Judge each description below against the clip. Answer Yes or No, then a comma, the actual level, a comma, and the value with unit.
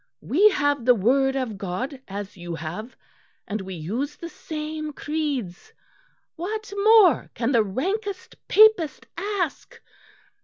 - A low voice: No, very high, 280 Hz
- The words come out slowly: Yes, slow, 125 wpm